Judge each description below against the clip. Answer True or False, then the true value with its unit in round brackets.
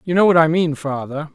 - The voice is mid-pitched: True (155 Hz)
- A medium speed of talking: False (265 wpm)